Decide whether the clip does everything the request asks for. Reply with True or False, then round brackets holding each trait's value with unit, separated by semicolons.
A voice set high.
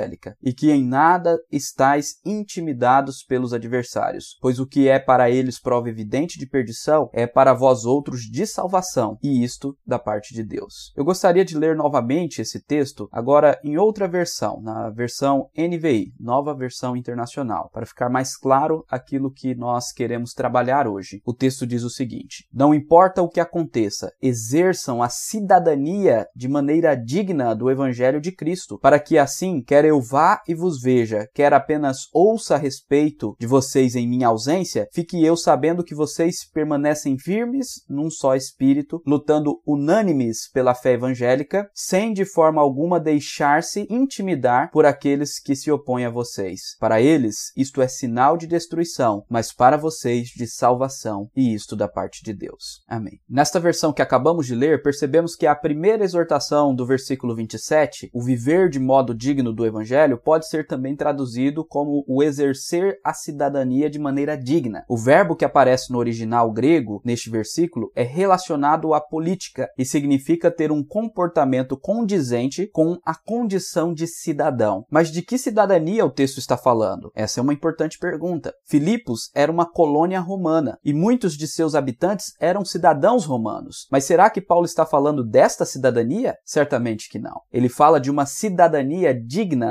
False (145 Hz)